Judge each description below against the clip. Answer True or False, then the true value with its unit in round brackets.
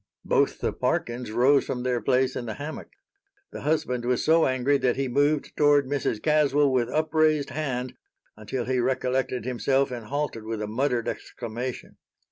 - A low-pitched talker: True (130 Hz)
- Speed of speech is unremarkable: True (165 wpm)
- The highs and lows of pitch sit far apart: False (2.8 semitones)